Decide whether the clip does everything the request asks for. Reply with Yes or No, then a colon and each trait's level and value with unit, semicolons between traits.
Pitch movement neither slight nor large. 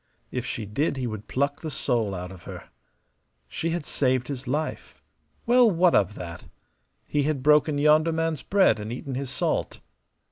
Yes: average, 5.0 semitones